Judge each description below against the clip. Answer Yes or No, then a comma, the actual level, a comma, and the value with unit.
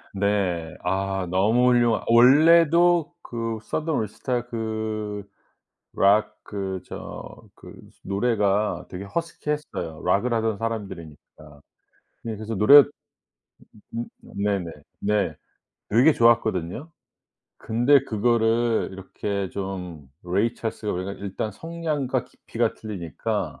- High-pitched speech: No, low, 110 Hz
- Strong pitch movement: No, average, 3.7 semitones